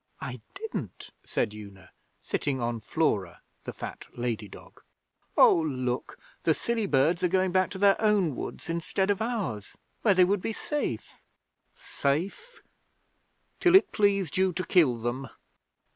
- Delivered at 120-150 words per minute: Yes, average, 145 wpm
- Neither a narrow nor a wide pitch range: No, wide, 8.2 semitones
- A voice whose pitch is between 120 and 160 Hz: No, medium, 170 Hz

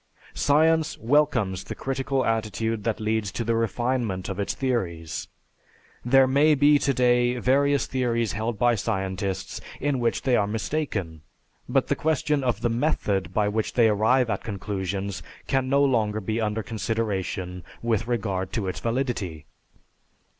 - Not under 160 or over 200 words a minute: No, average, 145 wpm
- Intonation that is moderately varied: Yes, average, 4.4 semitones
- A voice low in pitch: Yes, low, 115 Hz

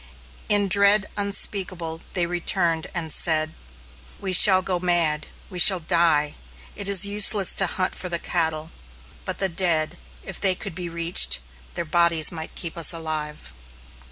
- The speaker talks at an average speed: Yes, average, 155 wpm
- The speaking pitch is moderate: Yes, medium, 175 Hz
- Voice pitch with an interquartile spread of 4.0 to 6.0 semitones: No, average, 2.8 semitones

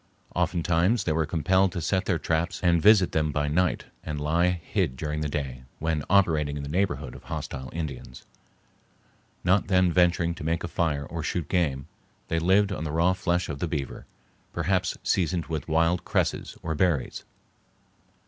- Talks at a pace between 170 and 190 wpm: Yes, average, 175 wpm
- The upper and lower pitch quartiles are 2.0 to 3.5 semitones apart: Yes, average, 3.0 semitones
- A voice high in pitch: No, very low, 85 Hz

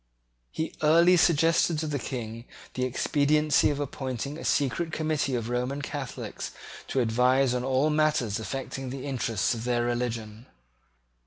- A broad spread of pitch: No, average, 3.8 semitones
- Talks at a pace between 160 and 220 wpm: No, average, 145 wpm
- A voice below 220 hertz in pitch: Yes, low, 135 Hz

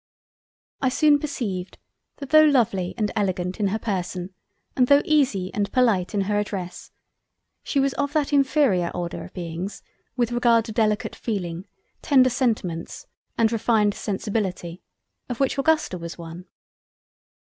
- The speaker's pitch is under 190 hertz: No, high, 210 Hz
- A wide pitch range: Yes, wide, 5.9 semitones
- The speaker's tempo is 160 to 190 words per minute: No, average, 145 wpm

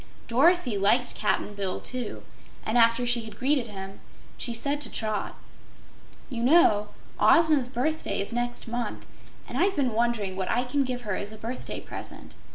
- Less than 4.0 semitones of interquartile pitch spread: Yes, average, 3.3 semitones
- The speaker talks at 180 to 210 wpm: No, average, 165 wpm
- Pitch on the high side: Yes, high, 240 Hz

